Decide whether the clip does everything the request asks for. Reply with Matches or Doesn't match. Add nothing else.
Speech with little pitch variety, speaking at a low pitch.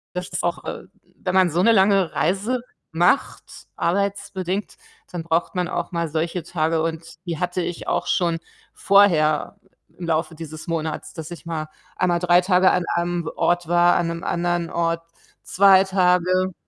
Doesn't match